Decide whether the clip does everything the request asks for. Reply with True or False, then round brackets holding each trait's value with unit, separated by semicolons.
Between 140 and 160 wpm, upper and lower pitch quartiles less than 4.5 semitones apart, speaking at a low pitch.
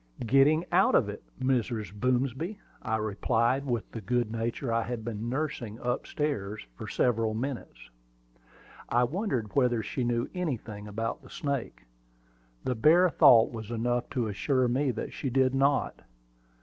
True (150 wpm; 3.3 semitones; 120 Hz)